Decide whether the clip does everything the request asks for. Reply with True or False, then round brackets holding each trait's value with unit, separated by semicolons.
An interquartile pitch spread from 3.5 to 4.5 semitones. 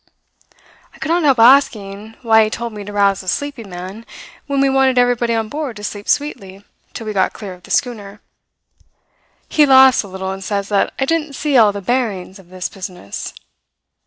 False (5.0 semitones)